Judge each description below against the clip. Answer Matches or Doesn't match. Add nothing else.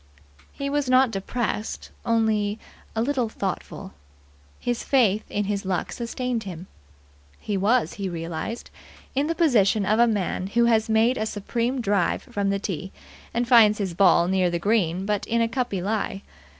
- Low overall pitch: Doesn't match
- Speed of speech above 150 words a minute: Matches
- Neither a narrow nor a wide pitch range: Matches